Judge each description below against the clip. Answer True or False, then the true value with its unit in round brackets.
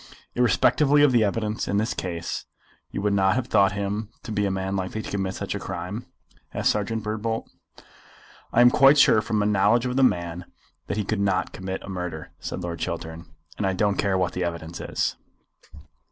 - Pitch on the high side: False (100 Hz)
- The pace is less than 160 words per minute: False (200 wpm)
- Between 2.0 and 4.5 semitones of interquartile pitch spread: True (2.9 semitones)